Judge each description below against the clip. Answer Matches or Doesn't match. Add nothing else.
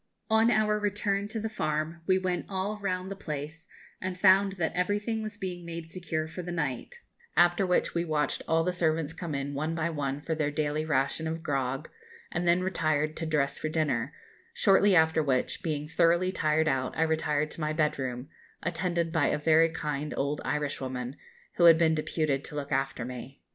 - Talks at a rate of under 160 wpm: Doesn't match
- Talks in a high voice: Doesn't match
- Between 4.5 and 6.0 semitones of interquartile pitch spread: Doesn't match